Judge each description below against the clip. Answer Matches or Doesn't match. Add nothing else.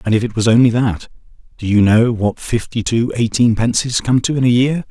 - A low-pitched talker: Matches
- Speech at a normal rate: Doesn't match